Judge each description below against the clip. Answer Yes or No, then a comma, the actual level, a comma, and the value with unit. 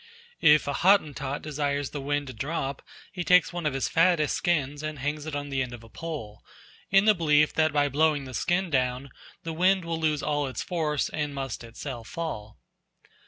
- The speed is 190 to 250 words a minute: Yes, average, 200 wpm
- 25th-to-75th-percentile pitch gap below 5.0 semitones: Yes, average, 3.0 semitones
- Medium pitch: Yes, medium, 150 Hz